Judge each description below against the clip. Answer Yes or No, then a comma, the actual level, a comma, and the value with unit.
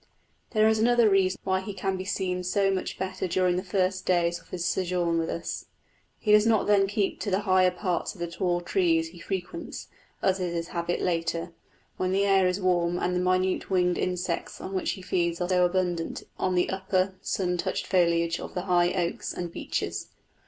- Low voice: No, medium, 185 Hz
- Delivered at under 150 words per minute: No, average, 200 wpm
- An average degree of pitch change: No, narrow, 1.6 semitones